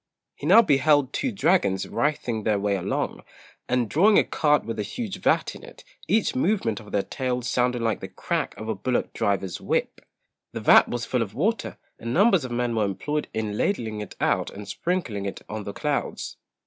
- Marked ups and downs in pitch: Yes, wide, 6.3 semitones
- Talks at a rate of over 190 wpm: Yes, average, 200 wpm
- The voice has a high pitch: No, low, 120 Hz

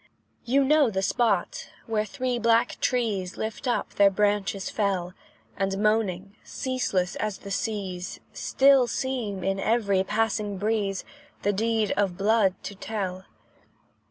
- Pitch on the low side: No, high, 210 Hz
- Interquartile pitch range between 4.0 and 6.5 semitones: No, average, 2.9 semitones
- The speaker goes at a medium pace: No, slow, 130 wpm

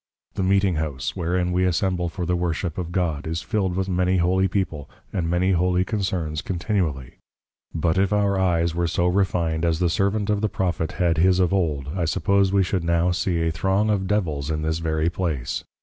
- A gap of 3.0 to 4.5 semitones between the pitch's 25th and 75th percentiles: No, narrow, 2.5 semitones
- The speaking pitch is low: Yes, very low, 90 Hz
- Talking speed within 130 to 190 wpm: No, average, 200 wpm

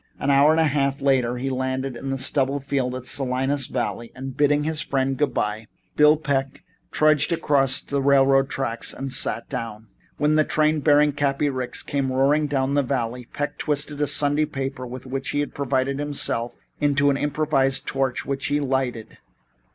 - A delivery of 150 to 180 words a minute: No, average, 190 wpm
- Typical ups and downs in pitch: No, narrow, 1.8 semitones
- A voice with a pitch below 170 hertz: Yes, low, 135 Hz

